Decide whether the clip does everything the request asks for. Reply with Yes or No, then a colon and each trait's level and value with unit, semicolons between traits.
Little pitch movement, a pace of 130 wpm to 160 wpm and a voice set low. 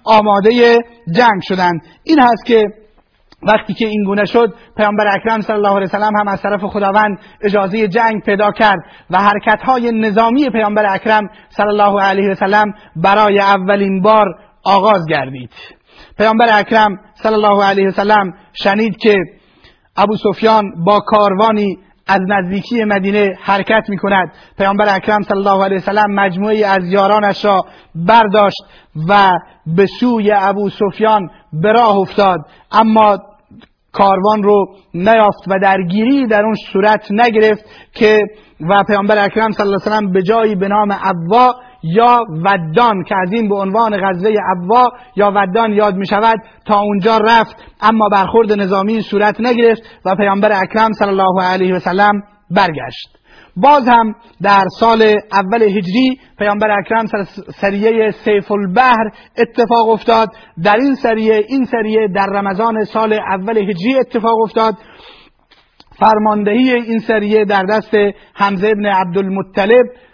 No: narrow, 2.0 semitones; average, 140 wpm; high, 210 Hz